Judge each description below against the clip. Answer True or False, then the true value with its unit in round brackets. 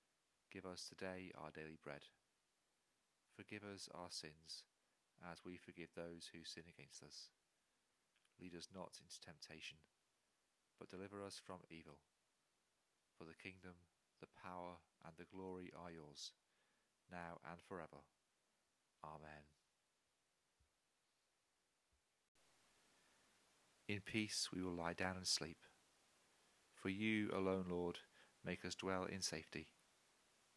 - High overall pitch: False (90 Hz)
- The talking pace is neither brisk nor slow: False (115 wpm)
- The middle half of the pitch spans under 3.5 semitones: True (2.8 semitones)